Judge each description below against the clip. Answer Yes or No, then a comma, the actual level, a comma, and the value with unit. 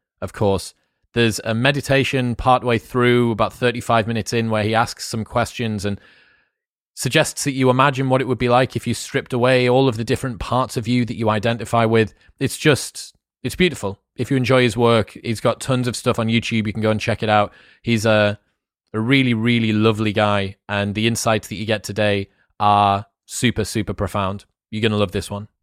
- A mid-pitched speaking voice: No, low, 115 Hz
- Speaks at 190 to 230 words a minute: Yes, fast, 205 wpm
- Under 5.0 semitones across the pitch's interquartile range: Yes, average, 2.8 semitones